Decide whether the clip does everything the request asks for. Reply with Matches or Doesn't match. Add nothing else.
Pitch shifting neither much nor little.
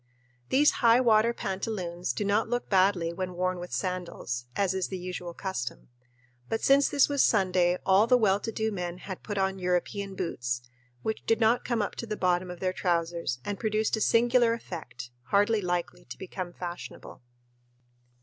Matches